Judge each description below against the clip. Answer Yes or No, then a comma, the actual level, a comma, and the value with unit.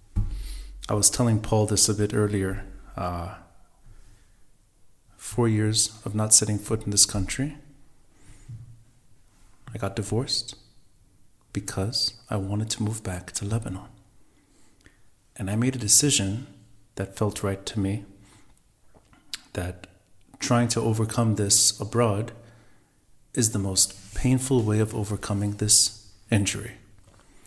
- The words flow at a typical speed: No, slow, 120 wpm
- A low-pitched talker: Yes, low, 105 Hz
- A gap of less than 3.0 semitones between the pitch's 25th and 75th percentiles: Yes, narrow, 2.4 semitones